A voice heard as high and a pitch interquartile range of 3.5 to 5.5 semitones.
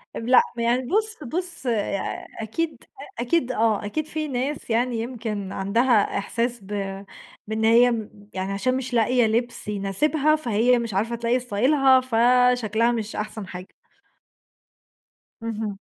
No: high, 235 Hz; average, 2.9 semitones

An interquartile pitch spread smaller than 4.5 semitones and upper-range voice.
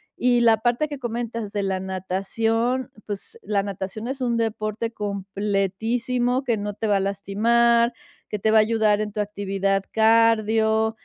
Yes: average, 2.7 semitones; high, 220 Hz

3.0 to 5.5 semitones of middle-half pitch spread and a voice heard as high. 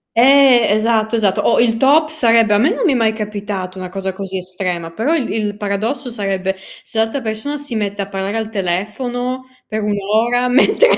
Yes: average, 3.7 semitones; high, 220 Hz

